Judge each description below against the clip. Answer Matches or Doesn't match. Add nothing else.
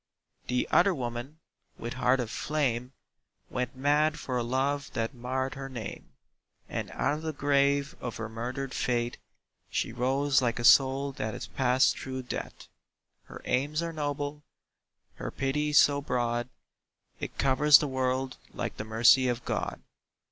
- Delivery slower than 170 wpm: Matches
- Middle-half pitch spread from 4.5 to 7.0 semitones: Doesn't match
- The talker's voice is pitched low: Matches